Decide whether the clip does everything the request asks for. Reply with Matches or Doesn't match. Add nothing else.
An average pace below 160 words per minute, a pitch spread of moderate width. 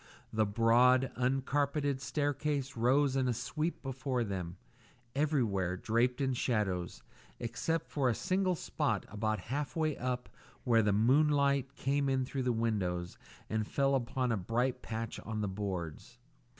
Matches